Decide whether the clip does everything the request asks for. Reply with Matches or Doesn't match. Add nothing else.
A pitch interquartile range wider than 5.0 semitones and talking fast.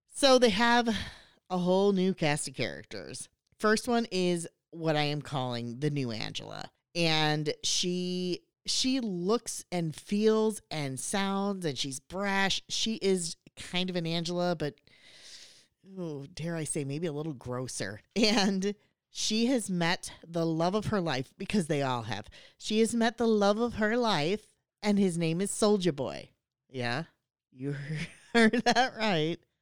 Doesn't match